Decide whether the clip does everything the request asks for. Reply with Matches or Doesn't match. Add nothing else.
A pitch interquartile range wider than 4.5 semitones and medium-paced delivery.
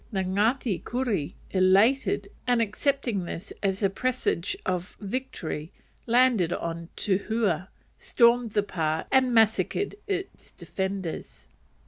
Doesn't match